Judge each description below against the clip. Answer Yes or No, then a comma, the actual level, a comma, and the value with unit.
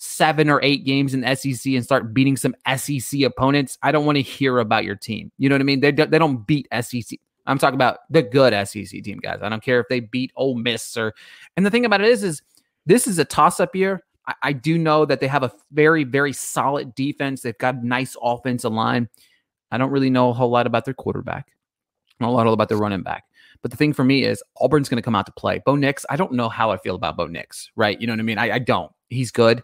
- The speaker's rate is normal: No, fast, 265 wpm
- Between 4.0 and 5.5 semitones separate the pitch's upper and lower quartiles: No, average, 3.0 semitones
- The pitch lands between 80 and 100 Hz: No, low, 130 Hz